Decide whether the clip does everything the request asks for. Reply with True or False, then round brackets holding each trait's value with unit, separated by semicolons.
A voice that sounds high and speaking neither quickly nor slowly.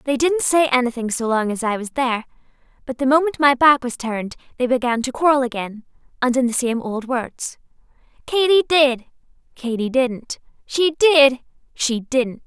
True (260 Hz; 170 wpm)